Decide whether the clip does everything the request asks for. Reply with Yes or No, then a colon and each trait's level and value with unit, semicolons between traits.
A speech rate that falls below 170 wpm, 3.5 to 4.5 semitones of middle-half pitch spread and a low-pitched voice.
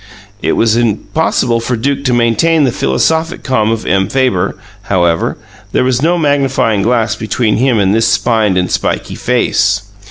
Yes: average, 160 wpm; average, 3.8 semitones; low, 115 Hz